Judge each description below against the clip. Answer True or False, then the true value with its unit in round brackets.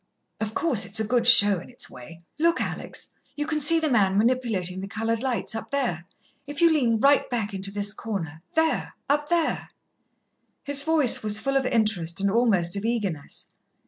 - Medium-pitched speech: False (225 Hz)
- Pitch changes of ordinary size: False (5.9 semitones)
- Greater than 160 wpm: True (185 wpm)